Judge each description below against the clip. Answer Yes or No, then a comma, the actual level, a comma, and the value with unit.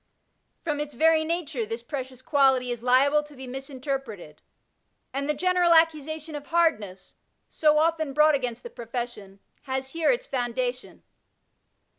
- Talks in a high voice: Yes, very high, 275 Hz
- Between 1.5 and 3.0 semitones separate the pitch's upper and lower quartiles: No, average, 4.0 semitones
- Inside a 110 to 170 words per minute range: Yes, average, 145 wpm